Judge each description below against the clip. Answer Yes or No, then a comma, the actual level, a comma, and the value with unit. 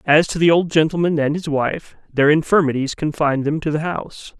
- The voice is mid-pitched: Yes, medium, 155 Hz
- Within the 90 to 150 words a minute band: No, fast, 205 wpm